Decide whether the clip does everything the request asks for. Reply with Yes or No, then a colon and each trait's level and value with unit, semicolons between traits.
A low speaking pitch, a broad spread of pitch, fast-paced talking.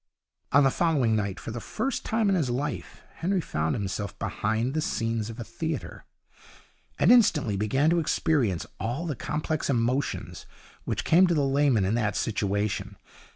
No: low, 130 Hz; wide, 6.4 semitones; average, 165 wpm